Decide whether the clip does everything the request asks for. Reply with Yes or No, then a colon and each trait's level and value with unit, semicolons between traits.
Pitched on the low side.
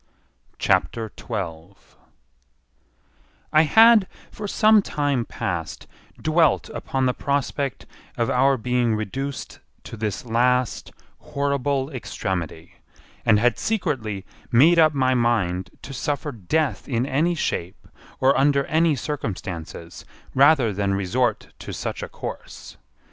Yes: low, 125 Hz